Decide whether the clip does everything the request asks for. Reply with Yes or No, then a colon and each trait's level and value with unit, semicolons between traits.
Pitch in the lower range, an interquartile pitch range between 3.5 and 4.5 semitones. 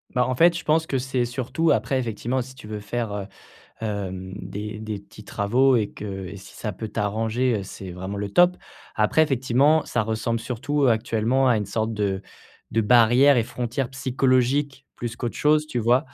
Yes: low, 120 Hz; average, 3.8 semitones